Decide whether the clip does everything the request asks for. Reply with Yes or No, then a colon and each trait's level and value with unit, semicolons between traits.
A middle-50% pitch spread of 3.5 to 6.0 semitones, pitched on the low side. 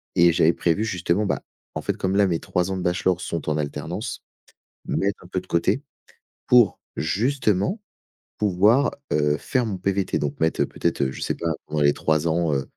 Yes: average, 3.9 semitones; very low, 90 Hz